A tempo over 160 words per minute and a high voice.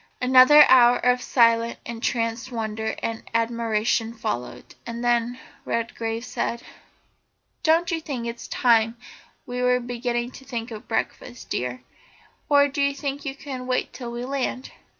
No: average, 150 wpm; high, 240 Hz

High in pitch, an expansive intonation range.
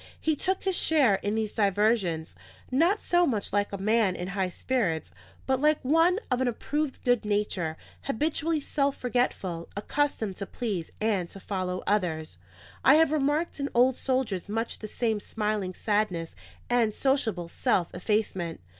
Yes: high, 220 Hz; wide, 6.0 semitones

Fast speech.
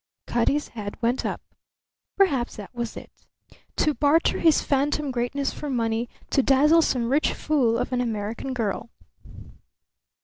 No: average, 140 wpm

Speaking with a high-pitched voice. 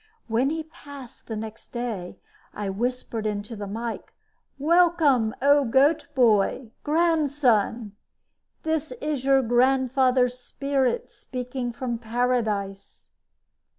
Yes: very high, 250 Hz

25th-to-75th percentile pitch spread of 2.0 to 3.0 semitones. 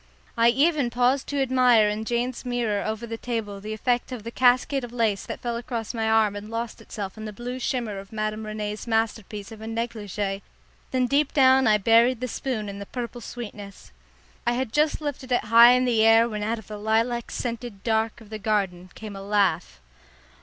Yes: narrow, 2.5 semitones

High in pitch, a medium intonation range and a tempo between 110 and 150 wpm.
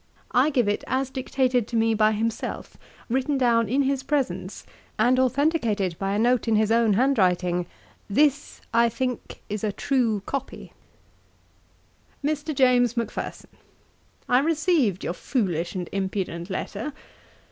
Yes: high, 235 Hz; average, 4.5 semitones; average, 140 wpm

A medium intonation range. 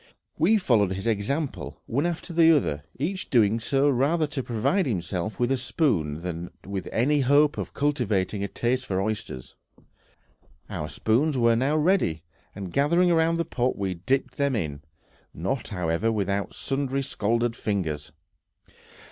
No: wide, 6.8 semitones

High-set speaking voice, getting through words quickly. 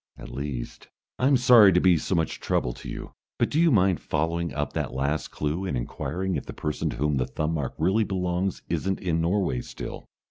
No: very low, 85 Hz; fast, 210 wpm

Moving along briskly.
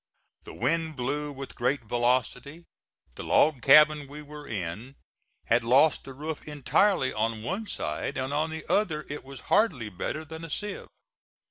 No: average, 160 wpm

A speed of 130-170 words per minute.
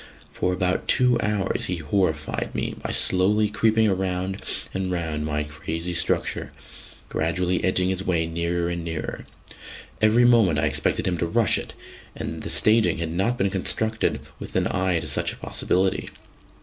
Yes: average, 160 wpm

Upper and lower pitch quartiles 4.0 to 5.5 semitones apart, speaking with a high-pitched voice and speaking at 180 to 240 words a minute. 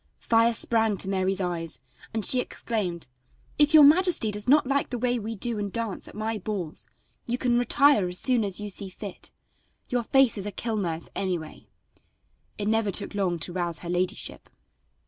Yes: average, 4.3 semitones; high, 210 Hz; average, 185 wpm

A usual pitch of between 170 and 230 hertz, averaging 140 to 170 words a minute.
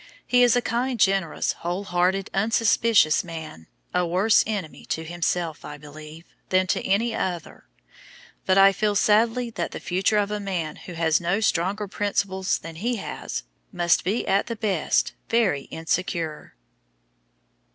Yes: high, 190 Hz; average, 150 wpm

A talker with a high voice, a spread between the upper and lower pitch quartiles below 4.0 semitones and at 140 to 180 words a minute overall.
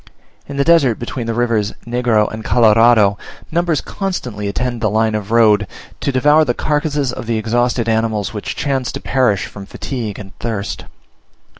No: low, 115 Hz; average, 3.4 semitones; average, 165 wpm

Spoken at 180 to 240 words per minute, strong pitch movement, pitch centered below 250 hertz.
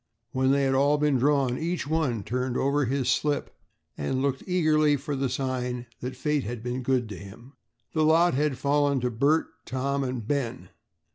No: average, 185 wpm; average, 2.8 semitones; low, 135 Hz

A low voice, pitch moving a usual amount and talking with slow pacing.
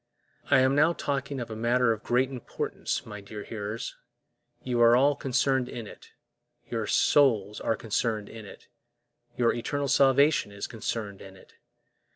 No: low, 120 Hz; average, 3.7 semitones; average, 160 wpm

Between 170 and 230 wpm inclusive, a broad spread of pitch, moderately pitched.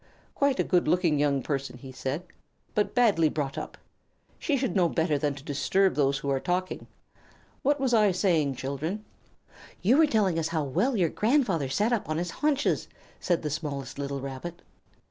Yes: average, 180 wpm; wide, 6.8 semitones; medium, 165 Hz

